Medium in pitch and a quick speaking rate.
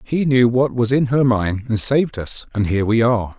No: low, 120 Hz; fast, 250 wpm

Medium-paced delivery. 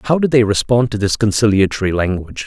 Yes: average, 195 wpm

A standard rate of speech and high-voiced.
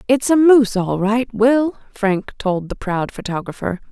Yes: average, 170 wpm; high, 220 Hz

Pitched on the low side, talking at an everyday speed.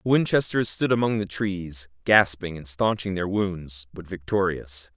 Yes: very low, 95 Hz; average, 155 wpm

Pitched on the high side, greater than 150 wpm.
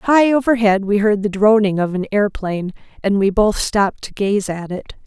Yes: high, 205 Hz; average, 200 wpm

